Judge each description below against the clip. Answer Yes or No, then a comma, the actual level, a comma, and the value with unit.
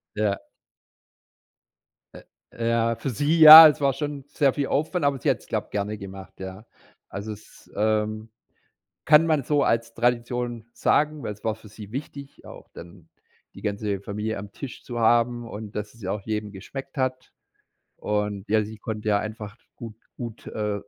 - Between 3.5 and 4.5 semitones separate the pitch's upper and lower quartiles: Yes, average, 4.2 semitones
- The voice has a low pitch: Yes, low, 110 Hz